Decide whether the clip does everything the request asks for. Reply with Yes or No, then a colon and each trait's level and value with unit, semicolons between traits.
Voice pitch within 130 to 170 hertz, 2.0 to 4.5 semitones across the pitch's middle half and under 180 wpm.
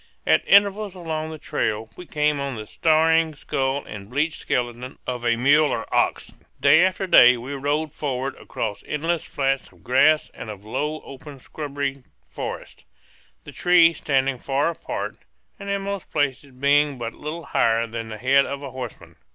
Yes: medium, 140 Hz; average, 3.8 semitones; average, 170 wpm